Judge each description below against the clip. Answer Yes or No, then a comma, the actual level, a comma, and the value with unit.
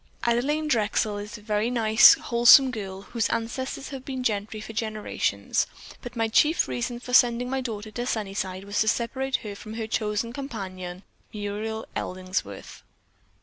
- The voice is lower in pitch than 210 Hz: No, high, 225 Hz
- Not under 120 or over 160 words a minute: Yes, average, 155 wpm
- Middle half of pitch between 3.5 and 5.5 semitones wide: No, average, 3.0 semitones